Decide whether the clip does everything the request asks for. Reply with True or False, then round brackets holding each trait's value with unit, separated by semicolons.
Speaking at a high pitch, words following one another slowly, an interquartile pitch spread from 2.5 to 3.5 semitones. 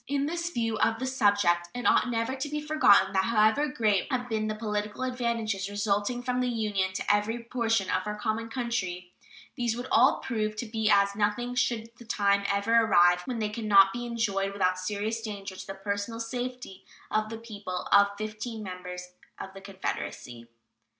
False (215 Hz; 190 wpm; 2.9 semitones)